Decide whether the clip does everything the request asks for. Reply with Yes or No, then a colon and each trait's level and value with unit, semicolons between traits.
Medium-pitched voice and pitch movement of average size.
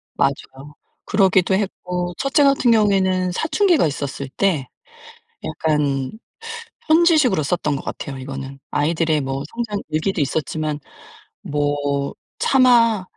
No: medium, 165 Hz; wide, 6.7 semitones